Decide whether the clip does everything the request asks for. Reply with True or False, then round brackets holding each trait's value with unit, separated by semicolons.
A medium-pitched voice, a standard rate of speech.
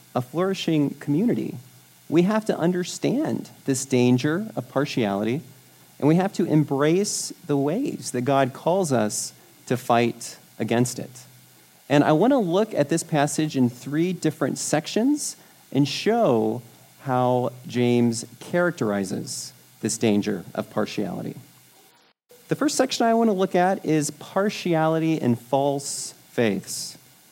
False (145 Hz; 130 wpm)